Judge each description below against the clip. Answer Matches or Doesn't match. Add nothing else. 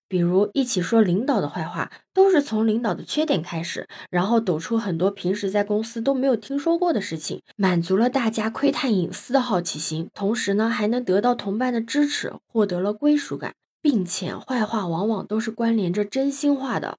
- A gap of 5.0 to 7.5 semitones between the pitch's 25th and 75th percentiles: Matches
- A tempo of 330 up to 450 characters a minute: Doesn't match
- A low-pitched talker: Doesn't match